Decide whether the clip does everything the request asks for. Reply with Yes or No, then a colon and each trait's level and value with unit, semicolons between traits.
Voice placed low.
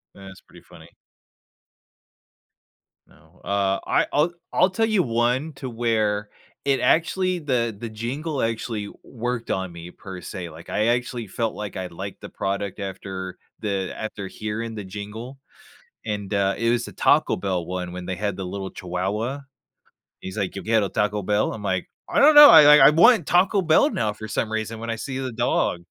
Yes: low, 110 Hz